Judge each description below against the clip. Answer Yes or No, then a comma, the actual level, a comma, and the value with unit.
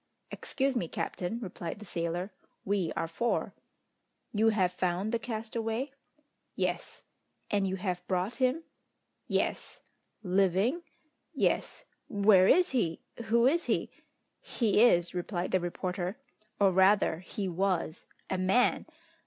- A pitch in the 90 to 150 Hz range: No, high, 195 Hz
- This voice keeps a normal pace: No, slow, 125 wpm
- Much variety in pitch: No, average, 3.9 semitones